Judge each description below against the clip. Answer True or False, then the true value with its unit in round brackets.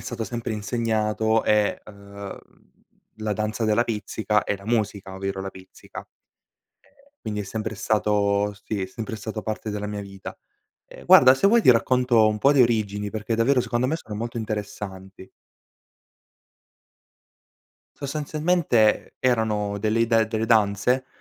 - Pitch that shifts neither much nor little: False (2.3 semitones)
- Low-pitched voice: True (110 Hz)